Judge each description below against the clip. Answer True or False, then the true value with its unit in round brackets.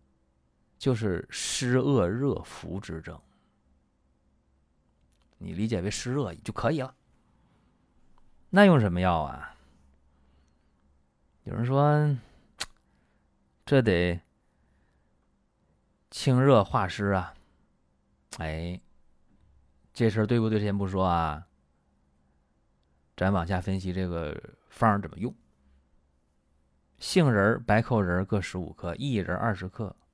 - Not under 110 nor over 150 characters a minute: True (140 characters per minute)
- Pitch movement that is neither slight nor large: False (7.5 semitones)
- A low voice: True (85 Hz)